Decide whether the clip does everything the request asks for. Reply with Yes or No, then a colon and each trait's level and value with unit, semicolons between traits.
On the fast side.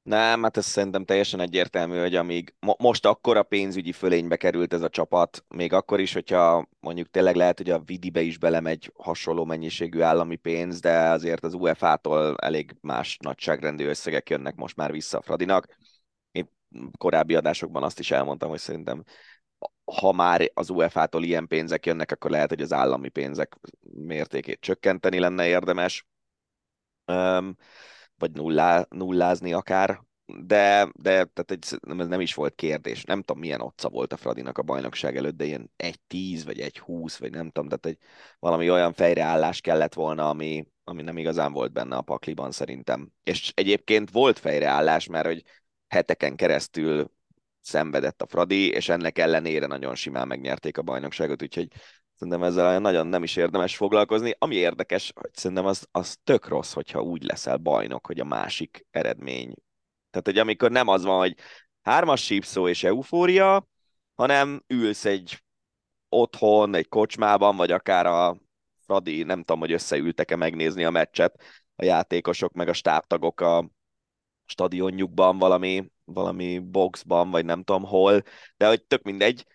Yes: fast, 160 wpm